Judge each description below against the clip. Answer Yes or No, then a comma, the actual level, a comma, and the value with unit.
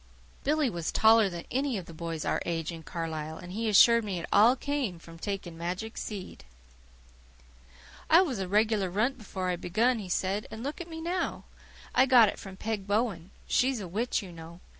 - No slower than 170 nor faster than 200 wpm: Yes, average, 195 wpm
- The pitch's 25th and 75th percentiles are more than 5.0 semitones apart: Yes, wide, 5.5 semitones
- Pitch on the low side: No, high, 205 Hz